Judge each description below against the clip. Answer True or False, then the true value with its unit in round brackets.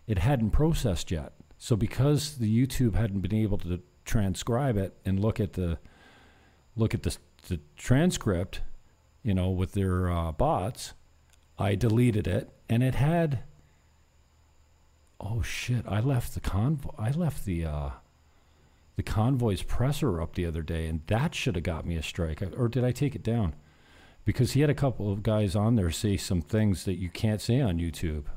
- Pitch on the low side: True (100 Hz)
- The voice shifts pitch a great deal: True (6.4 semitones)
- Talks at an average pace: True (180 wpm)